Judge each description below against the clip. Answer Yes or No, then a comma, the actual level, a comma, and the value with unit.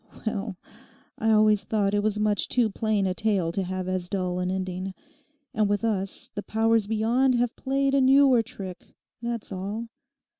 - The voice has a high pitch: Yes, high, 210 Hz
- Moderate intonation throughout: Yes, average, 3.2 semitones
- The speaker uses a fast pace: No, average, 175 wpm